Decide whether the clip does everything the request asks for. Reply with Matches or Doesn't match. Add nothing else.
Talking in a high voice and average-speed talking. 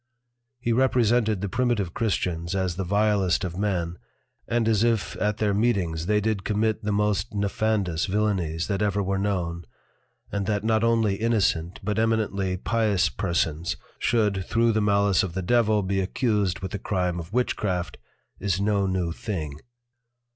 Doesn't match